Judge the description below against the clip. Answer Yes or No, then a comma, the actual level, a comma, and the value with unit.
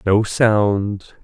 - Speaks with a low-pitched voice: Yes, low, 105 Hz